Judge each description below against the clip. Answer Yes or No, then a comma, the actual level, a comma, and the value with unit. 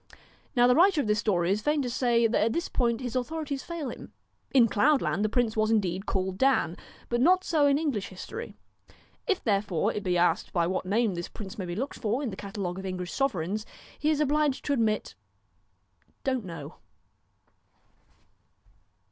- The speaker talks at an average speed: Yes, average, 190 wpm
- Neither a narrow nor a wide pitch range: No, wide, 6.3 semitones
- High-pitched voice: Yes, high, 225 Hz